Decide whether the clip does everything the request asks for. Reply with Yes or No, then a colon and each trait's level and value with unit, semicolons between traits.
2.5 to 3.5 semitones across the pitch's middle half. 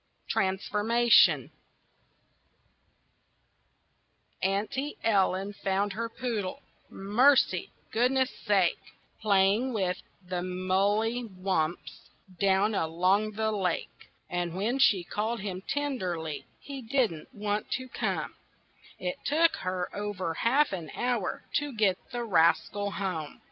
No: average, 4.1 semitones